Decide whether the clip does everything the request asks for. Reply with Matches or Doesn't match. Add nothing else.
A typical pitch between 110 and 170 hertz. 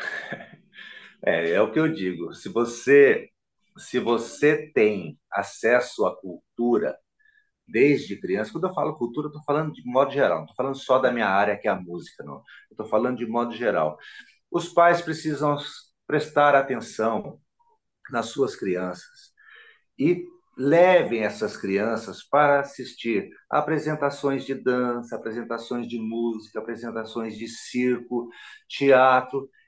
Matches